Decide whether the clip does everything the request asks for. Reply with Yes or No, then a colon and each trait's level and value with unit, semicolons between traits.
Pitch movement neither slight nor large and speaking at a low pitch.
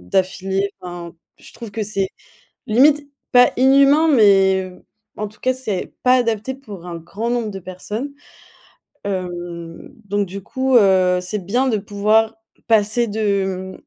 No: average, 4.2 semitones; high, 205 Hz